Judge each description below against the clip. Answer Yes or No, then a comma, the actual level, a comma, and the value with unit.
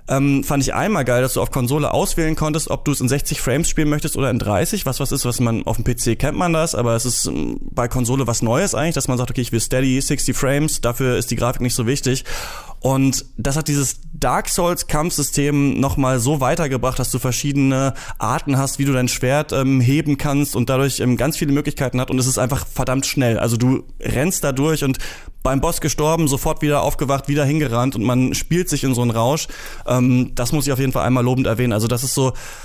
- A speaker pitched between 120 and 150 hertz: Yes, low, 135 Hz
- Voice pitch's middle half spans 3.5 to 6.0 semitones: No, narrow, 2.6 semitones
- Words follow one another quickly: Yes, fast, 235 wpm